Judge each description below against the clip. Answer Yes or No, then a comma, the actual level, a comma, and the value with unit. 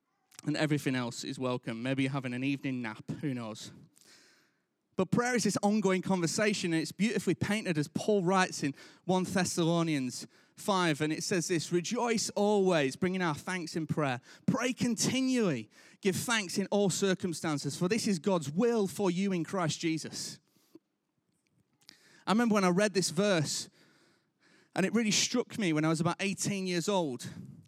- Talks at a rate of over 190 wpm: No, average, 165 wpm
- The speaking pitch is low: No, medium, 180 Hz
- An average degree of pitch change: Yes, average, 4.7 semitones